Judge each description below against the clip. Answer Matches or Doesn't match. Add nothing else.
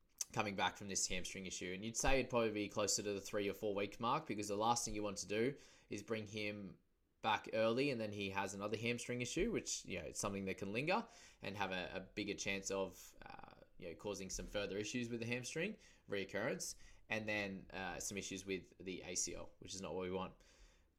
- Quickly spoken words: Matches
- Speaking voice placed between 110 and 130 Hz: Doesn't match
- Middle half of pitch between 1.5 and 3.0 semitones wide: Matches